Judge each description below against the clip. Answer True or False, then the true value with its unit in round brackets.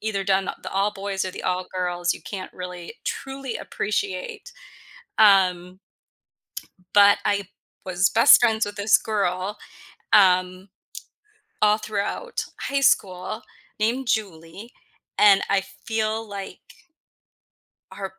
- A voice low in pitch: False (200 Hz)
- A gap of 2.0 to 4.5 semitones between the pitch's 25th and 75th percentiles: True (3.0 semitones)